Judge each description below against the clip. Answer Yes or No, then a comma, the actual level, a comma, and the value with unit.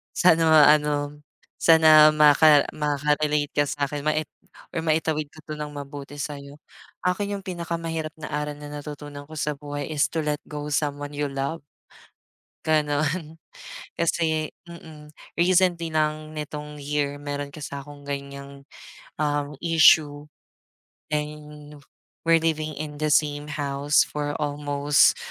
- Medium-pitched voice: Yes, medium, 150 Hz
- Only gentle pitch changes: Yes, narrow, 1.3 semitones